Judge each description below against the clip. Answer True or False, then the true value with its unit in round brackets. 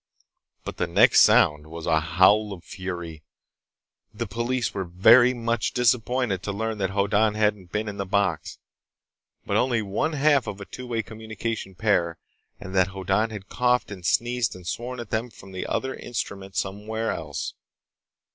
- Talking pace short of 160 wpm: False (165 wpm)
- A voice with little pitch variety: False (3.7 semitones)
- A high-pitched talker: False (105 Hz)